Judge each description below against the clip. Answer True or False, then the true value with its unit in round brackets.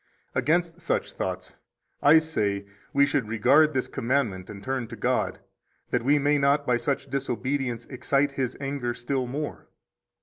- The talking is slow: False (160 wpm)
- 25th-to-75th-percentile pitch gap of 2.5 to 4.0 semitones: True (2.9 semitones)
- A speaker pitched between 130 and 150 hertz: True (135 Hz)